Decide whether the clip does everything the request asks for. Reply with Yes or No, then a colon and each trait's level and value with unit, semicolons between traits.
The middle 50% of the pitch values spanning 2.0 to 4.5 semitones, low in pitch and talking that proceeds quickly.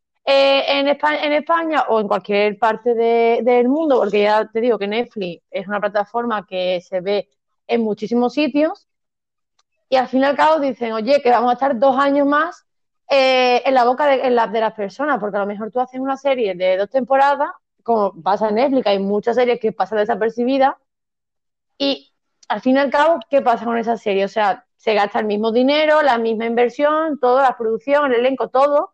No: average, 4.2 semitones; high, 245 Hz; fast, 210 wpm